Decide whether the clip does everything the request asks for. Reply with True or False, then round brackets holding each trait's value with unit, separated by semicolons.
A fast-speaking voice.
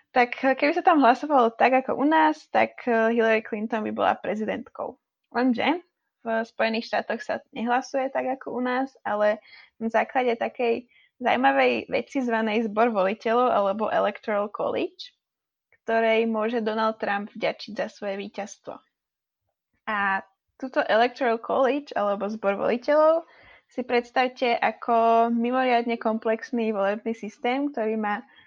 False (130 wpm)